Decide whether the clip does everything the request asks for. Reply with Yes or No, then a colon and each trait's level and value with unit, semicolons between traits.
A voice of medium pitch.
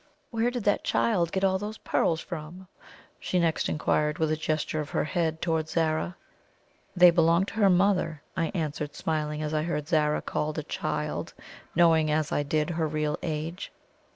Yes: medium, 160 Hz